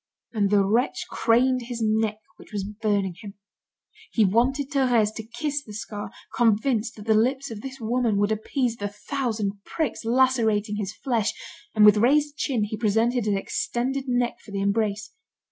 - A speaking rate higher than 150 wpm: Yes, average, 170 wpm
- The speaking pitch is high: Yes, high, 225 Hz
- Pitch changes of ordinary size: Yes, average, 3.3 semitones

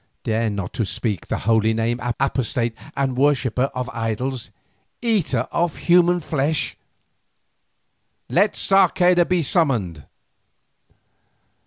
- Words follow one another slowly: Yes, slow, 105 wpm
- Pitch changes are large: Yes, wide, 7.1 semitones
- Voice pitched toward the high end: No, low, 130 Hz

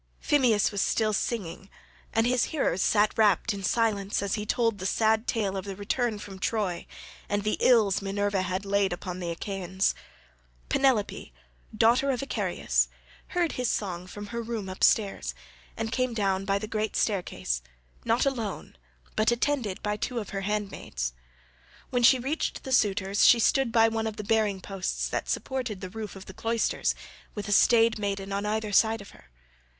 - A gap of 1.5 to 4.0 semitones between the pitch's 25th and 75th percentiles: Yes, average, 2.7 semitones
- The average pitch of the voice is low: No, high, 210 Hz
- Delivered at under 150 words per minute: No, average, 175 wpm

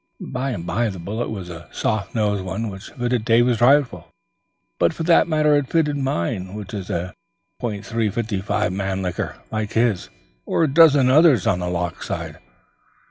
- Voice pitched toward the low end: Yes, low, 110 Hz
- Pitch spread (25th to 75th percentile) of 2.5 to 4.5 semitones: No, wide, 5.6 semitones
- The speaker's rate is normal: Yes, average, 165 wpm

